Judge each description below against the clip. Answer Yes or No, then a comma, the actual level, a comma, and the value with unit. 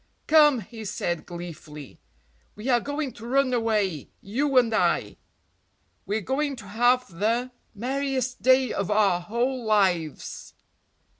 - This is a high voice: Yes, high, 230 Hz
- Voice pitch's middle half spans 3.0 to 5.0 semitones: Yes, average, 4.5 semitones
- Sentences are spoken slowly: Yes, slow, 130 wpm